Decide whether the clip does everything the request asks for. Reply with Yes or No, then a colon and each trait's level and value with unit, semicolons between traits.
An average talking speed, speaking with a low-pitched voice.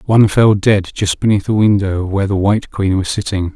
No: fast, 220 wpm; low, 100 Hz